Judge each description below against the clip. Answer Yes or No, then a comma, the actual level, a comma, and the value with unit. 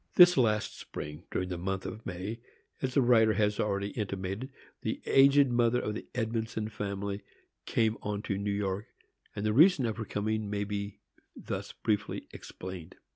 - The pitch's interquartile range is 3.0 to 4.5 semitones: No, narrow, 2.5 semitones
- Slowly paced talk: No, average, 170 wpm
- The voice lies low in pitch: Yes, low, 105 Hz